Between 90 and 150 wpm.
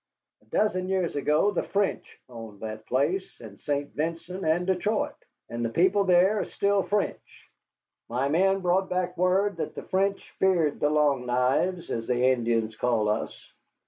No: average, 165 wpm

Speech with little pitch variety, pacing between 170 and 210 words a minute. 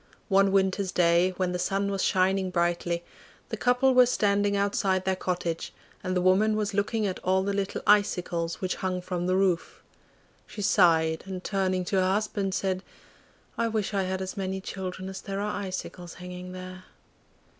Yes: narrow, 1.6 semitones; average, 175 wpm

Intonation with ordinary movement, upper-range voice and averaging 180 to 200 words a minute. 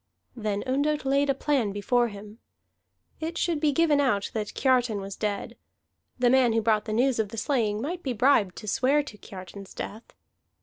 Yes: average, 5.0 semitones; high, 240 Hz; average, 185 wpm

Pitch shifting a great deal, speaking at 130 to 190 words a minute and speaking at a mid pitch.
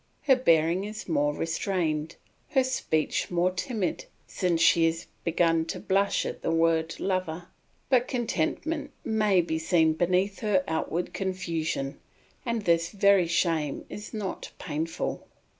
No: average, 3.6 semitones; slow, 135 wpm; medium, 175 Hz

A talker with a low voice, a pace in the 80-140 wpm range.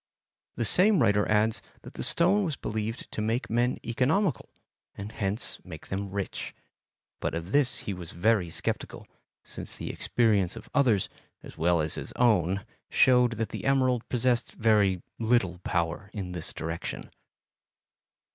No: low, 110 Hz; average, 155 wpm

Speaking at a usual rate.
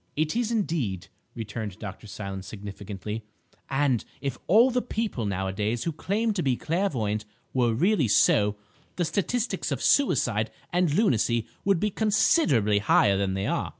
Yes: average, 150 wpm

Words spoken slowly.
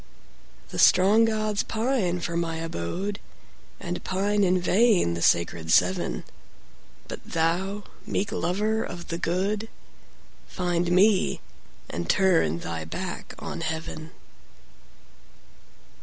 Yes: slow, 95 wpm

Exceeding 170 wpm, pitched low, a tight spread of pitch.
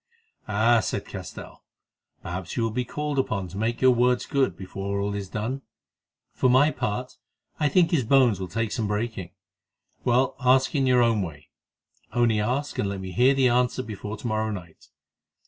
No: average, 180 wpm; low, 115 Hz; average, 3.9 semitones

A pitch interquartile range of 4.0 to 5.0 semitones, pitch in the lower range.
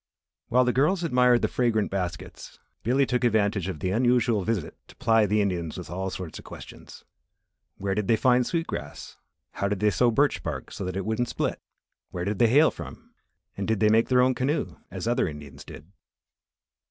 Yes: average, 4.5 semitones; low, 110 Hz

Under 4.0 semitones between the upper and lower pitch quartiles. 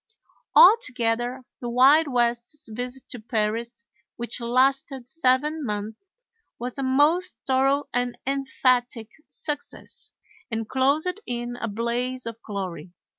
Yes: narrow, 2.6 semitones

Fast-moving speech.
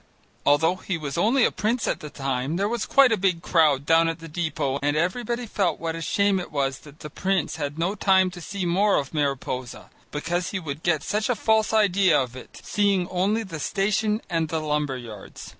Yes: fast, 215 wpm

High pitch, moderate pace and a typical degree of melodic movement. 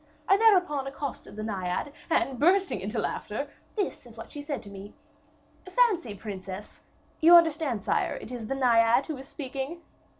No: very high, 270 Hz; average, 165 wpm; wide, 6.9 semitones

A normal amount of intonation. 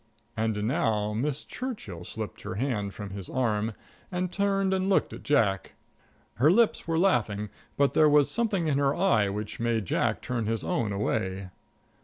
No: wide, 7.8 semitones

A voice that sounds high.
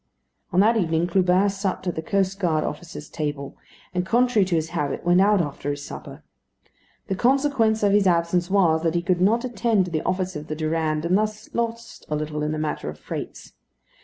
No: medium, 180 Hz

